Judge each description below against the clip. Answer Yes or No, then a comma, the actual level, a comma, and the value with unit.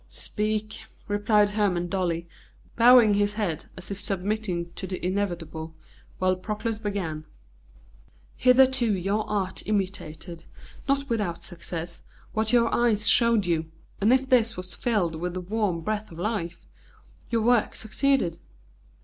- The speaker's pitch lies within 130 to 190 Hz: No, high, 205 Hz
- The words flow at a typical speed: No, slow, 130 wpm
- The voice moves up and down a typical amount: Yes, average, 3.9 semitones